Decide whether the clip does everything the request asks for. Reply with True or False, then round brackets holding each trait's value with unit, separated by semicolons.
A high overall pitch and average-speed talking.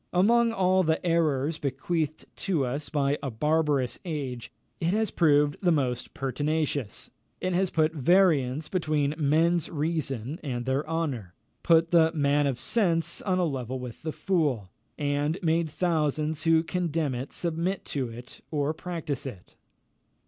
False (155 Hz; 150 wpm)